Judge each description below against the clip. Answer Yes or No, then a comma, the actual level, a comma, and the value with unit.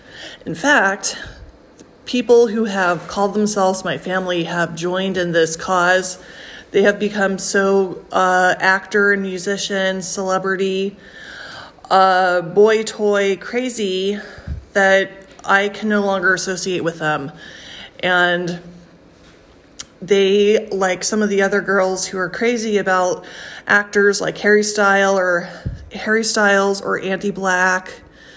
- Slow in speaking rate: Yes, slow, 115 wpm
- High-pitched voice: Yes, high, 195 Hz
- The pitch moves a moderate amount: No, narrow, 1.8 semitones